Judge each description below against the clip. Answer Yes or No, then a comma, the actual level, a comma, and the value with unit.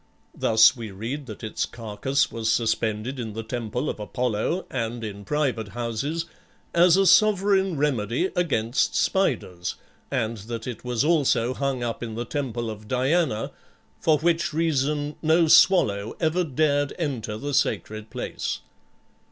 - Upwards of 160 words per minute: No, average, 145 wpm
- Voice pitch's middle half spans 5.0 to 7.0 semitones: Yes, wide, 5.6 semitones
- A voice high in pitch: No, low, 125 Hz